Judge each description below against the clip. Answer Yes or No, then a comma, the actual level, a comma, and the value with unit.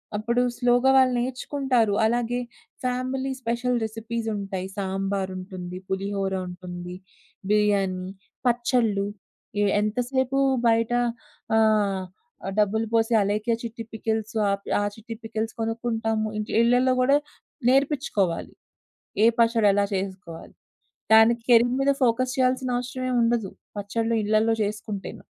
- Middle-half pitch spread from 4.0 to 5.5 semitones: No, average, 3.3 semitones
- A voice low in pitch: No, high, 225 Hz